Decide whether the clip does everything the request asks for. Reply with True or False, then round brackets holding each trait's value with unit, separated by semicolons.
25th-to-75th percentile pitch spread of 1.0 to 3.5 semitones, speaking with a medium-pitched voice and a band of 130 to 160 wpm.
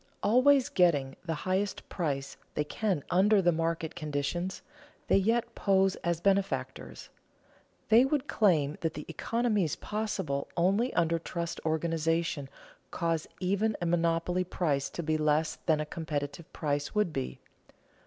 False (4.1 semitones; 170 Hz; 135 wpm)